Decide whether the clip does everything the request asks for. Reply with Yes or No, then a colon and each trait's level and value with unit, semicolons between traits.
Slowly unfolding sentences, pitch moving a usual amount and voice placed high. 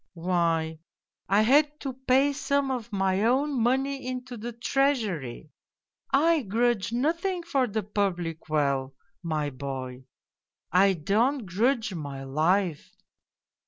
No: slow, 125 wpm; wide, 8.3 semitones; high, 215 Hz